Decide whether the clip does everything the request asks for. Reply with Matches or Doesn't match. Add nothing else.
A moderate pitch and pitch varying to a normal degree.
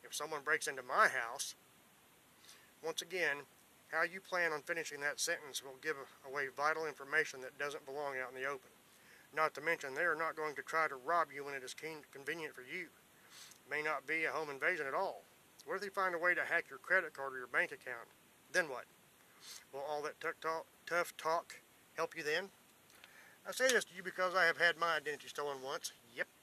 Matches